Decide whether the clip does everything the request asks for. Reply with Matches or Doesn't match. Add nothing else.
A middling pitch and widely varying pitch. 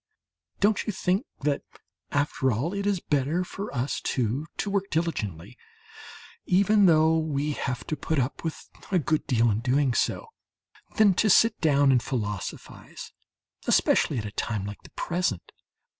Matches